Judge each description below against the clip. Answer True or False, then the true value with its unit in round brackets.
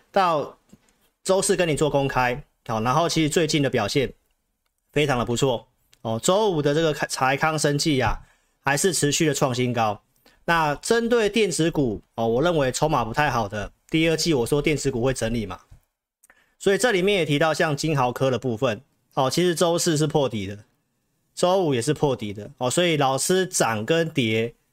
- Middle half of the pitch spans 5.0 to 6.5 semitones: False (4.6 semitones)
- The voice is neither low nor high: True (145 Hz)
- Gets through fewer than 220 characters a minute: False (270 characters per minute)